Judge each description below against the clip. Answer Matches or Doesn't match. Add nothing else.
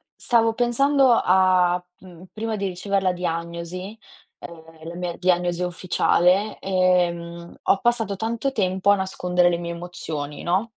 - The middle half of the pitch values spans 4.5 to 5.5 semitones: Doesn't match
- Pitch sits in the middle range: Matches